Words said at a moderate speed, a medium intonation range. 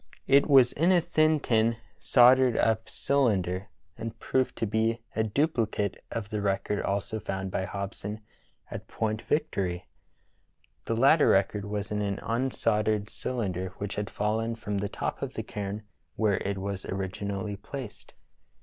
Yes: average, 160 wpm; average, 3.0 semitones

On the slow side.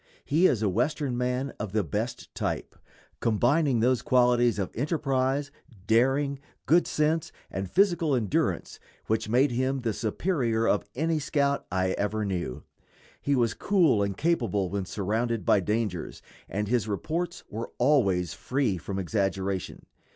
No: average, 145 wpm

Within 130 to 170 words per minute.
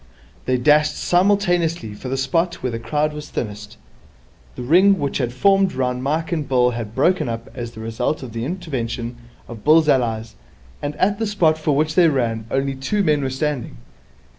No: average, 190 wpm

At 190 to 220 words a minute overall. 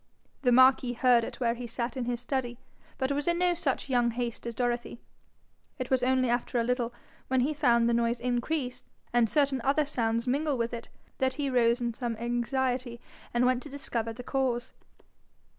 Yes: average, 195 wpm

